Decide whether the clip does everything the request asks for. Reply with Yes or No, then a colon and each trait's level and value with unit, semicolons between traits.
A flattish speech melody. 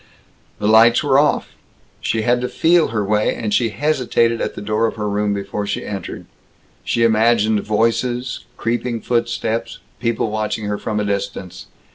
Yes: narrow, 2.1 semitones